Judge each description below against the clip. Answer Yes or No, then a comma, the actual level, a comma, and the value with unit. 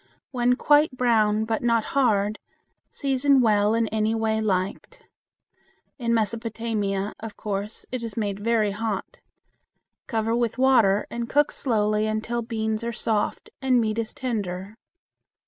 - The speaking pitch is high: Yes, high, 225 Hz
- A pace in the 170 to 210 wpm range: No, slow, 135 wpm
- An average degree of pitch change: No, narrow, 2.1 semitones